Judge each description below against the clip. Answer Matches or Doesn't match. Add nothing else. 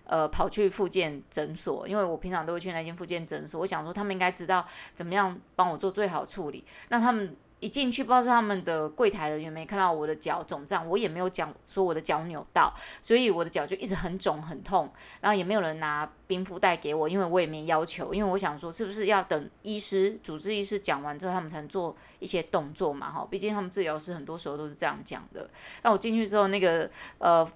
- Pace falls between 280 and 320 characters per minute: Doesn't match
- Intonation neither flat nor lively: Matches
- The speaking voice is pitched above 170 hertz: Matches